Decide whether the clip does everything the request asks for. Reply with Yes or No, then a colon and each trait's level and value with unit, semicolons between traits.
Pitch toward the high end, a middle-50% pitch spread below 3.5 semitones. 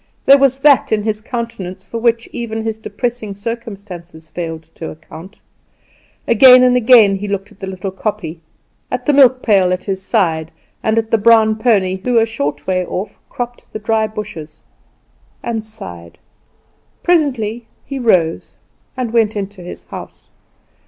No: high, 215 Hz; average, 3.8 semitones